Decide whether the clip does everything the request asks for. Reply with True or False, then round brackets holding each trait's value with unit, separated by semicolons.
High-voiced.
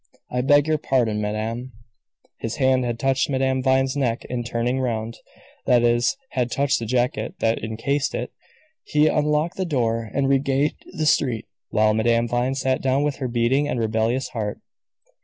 False (125 Hz)